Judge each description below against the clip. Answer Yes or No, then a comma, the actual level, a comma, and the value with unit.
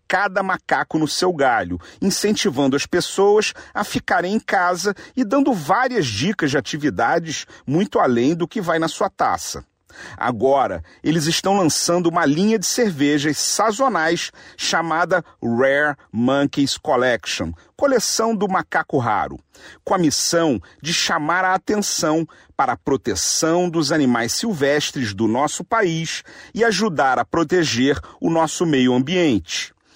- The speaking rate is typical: Yes, average, 135 wpm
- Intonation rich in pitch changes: Yes, wide, 5.9 semitones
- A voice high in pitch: No, medium, 170 Hz